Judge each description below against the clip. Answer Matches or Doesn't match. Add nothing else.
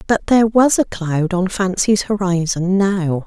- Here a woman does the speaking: Matches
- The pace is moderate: Matches